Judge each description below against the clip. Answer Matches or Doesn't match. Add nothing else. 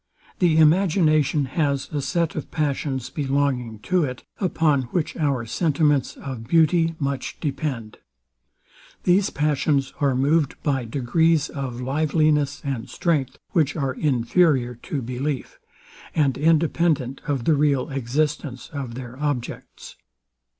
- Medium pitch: Matches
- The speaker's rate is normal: Doesn't match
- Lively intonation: Doesn't match